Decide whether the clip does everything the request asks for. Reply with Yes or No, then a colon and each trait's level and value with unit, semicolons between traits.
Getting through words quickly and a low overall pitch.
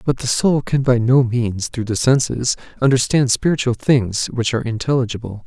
No: average, 175 wpm; low, 125 Hz